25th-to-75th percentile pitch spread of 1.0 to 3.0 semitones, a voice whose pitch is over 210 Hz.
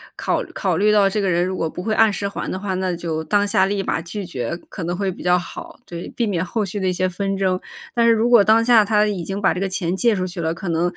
No: narrow, 2.6 semitones; high, 190 Hz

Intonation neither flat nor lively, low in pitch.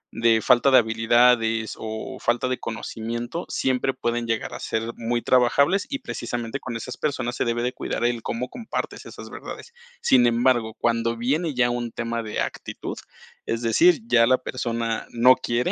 No: narrow, 1.8 semitones; low, 120 Hz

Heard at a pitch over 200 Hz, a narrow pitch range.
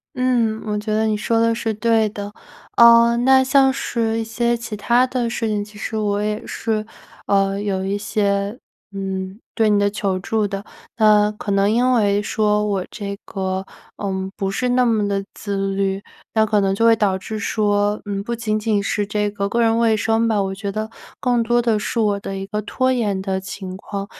Yes: high, 210 Hz; narrow, 2.3 semitones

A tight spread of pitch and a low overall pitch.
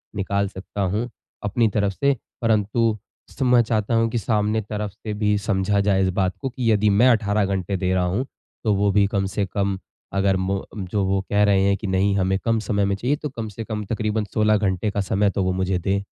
Yes: narrow, 1.9 semitones; low, 100 Hz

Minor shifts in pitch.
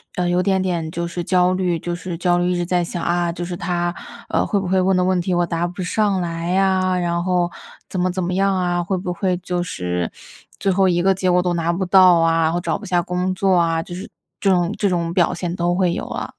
Yes: narrow, 1.3 semitones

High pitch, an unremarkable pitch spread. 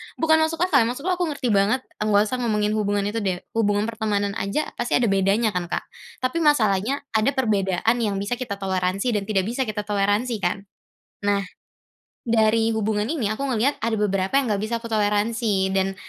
Yes: high, 215 Hz; average, 3.2 semitones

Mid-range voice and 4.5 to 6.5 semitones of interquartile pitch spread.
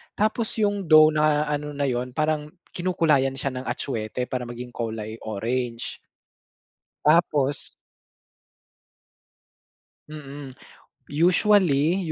No: medium, 145 Hz; average, 3.8 semitones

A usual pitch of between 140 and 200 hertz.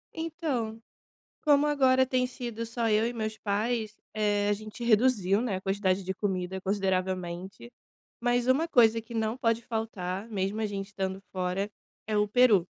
No: high, 215 Hz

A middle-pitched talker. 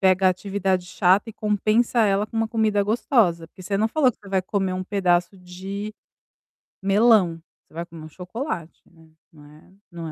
No: high, 195 Hz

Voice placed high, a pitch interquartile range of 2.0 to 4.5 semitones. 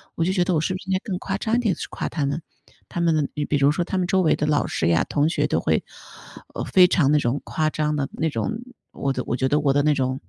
No: medium, 155 Hz; average, 4.1 semitones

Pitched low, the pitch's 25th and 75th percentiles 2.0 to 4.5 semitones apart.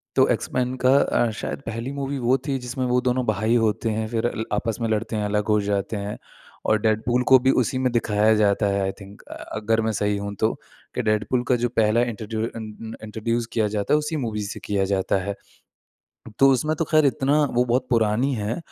Yes: low, 115 Hz; average, 3.0 semitones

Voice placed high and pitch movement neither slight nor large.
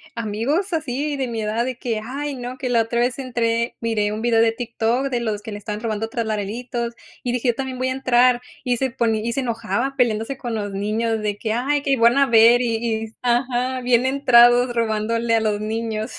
No: high, 235 Hz; narrow, 2.2 semitones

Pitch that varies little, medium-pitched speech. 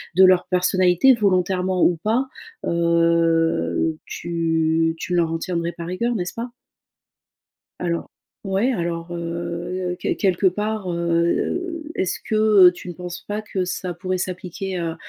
Yes: narrow, 2.2 semitones; medium, 180 Hz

